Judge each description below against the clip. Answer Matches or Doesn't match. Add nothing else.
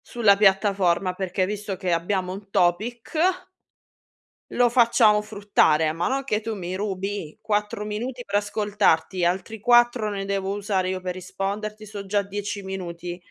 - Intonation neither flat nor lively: Doesn't match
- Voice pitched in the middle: Doesn't match